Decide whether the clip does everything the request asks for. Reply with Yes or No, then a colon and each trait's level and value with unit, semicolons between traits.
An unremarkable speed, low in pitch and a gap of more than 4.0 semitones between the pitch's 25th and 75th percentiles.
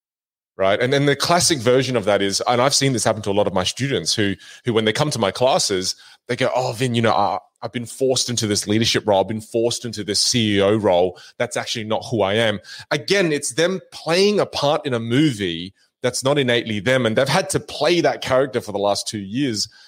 No: fast, 240 wpm; low, 120 Hz; average, 5.1 semitones